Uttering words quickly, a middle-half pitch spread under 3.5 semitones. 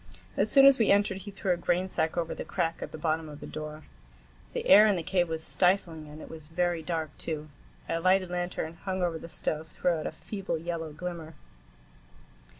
Yes: fast, 210 wpm; average, 2.7 semitones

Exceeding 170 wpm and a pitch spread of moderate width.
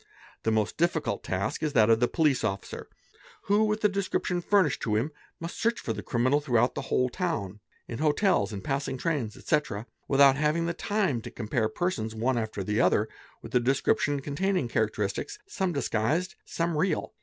No: average, 190 wpm; wide, 7.3 semitones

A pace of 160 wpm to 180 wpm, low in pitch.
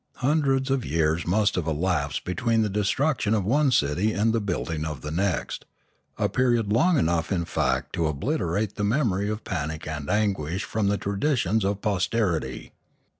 Yes: average, 170 wpm; low, 100 Hz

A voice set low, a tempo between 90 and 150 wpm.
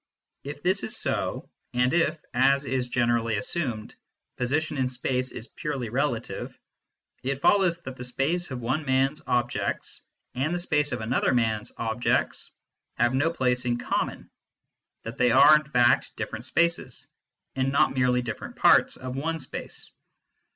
No: low, 130 Hz; average, 160 wpm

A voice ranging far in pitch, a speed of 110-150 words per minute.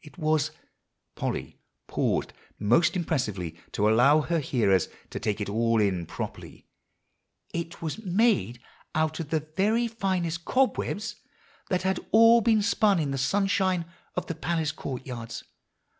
Yes: wide, 7.9 semitones; average, 145 wpm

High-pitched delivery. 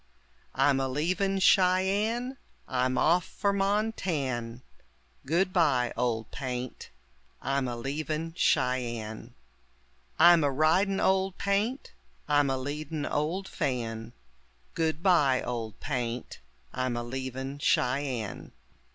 No: medium, 145 Hz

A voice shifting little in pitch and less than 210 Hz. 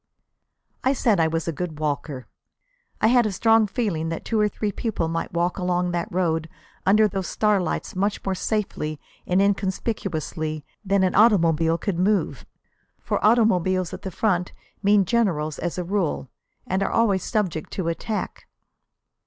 No: average, 4.0 semitones; medium, 185 Hz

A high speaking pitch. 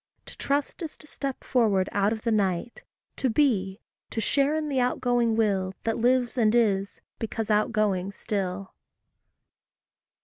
Yes: high, 225 Hz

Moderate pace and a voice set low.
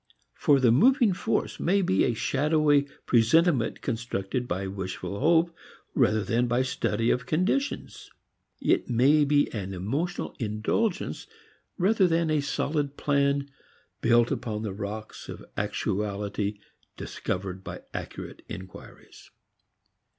No: slow, 120 wpm; low, 125 Hz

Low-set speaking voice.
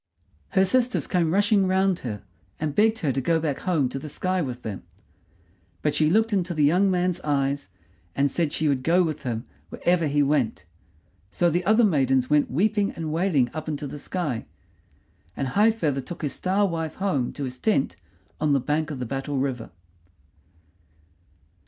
No: medium, 155 Hz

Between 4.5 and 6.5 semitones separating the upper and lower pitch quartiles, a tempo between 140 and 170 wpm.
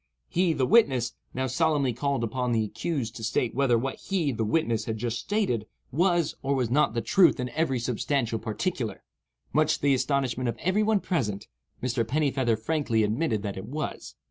No: average, 5.0 semitones; average, 185 wpm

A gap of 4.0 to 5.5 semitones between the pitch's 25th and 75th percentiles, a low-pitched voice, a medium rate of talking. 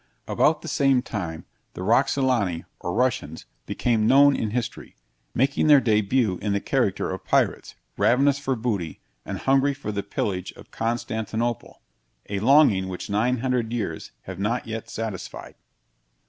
Yes: average, 4.5 semitones; low, 115 Hz; average, 145 wpm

